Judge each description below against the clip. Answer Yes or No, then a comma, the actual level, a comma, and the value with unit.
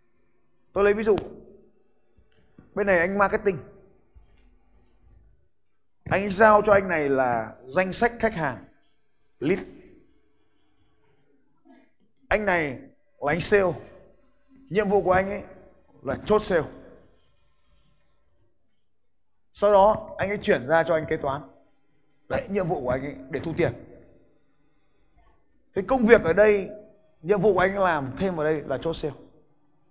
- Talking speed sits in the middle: No, slow, 135 wpm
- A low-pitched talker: No, medium, 180 Hz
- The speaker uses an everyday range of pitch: No, wide, 6.2 semitones